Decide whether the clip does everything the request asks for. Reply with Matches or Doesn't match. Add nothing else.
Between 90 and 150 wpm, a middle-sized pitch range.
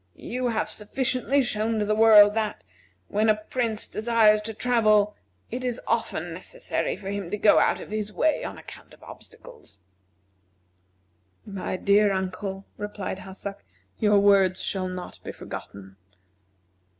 Doesn't match